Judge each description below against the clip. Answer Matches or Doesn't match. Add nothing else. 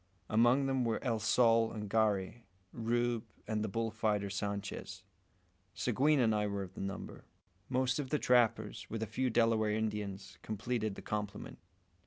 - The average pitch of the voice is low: Matches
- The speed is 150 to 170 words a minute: Matches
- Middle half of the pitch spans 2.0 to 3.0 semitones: Matches